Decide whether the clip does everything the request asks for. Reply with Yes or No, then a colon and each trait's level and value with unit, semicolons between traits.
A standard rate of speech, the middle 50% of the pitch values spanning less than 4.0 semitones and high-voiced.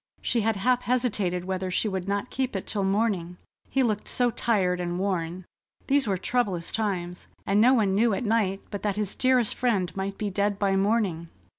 Yes: average, 195 wpm; average, 3.5 semitones; high, 200 Hz